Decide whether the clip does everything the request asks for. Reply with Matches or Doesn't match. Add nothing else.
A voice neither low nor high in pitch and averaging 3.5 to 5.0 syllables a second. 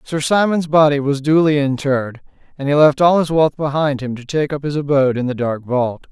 Doesn't match